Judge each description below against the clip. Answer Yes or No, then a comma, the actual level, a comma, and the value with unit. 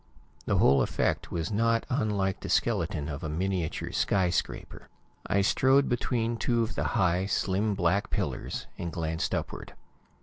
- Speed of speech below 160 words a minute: Yes, average, 145 wpm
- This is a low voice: Yes, very low, 95 Hz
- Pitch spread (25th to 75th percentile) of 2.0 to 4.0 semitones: No, average, 5.1 semitones